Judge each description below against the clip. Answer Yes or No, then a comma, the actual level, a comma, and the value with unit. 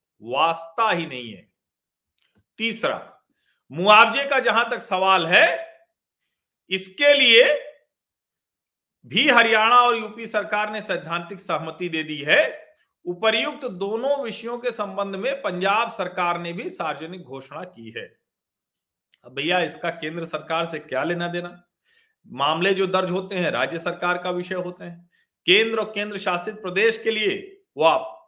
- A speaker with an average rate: Yes, average, 135 wpm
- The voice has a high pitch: Yes, high, 195 Hz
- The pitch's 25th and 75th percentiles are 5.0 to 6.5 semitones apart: Yes, wide, 5.5 semitones